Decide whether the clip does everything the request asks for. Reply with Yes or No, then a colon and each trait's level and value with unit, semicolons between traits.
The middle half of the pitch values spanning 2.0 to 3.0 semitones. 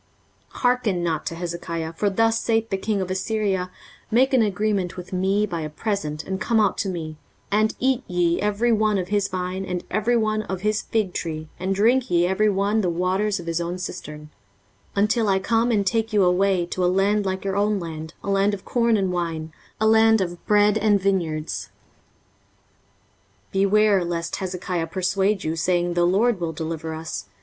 No: average, 3.4 semitones